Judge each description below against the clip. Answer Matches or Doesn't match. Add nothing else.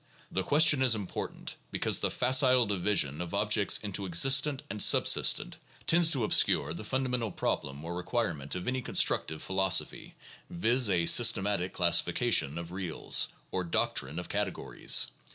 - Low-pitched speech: Matches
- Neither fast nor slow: Matches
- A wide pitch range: Matches